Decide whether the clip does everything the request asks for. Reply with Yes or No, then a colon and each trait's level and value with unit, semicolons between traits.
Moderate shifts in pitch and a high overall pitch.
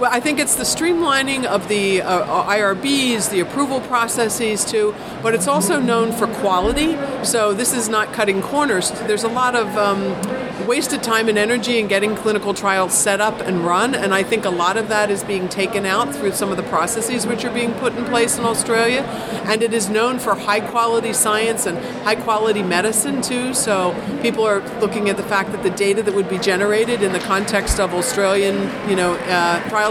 Yes: average, 3.0 semitones; high, 215 Hz